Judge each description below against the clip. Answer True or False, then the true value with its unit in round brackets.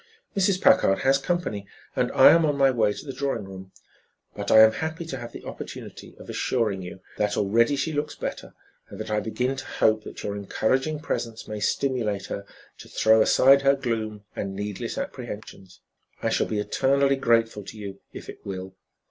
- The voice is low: True (115 Hz)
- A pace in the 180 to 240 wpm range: True (190 wpm)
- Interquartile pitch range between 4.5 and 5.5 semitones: True (5.0 semitones)